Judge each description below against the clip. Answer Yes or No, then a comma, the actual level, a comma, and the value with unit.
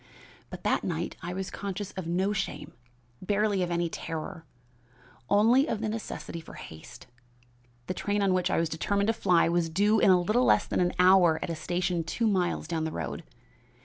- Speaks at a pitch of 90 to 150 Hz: No, medium, 185 Hz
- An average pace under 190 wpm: No, average, 195 wpm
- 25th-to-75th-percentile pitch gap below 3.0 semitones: No, average, 3.4 semitones